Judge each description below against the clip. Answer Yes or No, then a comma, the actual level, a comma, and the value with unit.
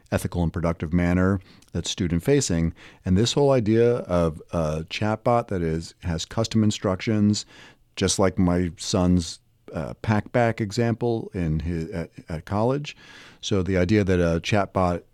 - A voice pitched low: Yes, very low, 95 Hz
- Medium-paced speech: Yes, average, 145 wpm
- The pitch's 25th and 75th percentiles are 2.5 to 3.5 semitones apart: No, average, 4.6 semitones